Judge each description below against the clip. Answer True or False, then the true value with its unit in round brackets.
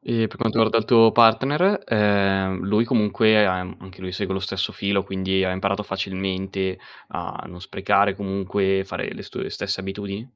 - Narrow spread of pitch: True (2.3 semitones)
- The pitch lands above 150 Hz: False (100 Hz)